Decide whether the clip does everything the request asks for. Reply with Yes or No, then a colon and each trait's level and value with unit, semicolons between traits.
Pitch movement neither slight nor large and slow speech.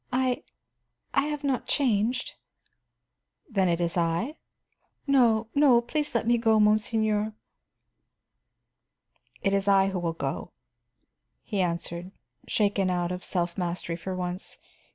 Yes: average, 4.9 semitones; slow, 125 wpm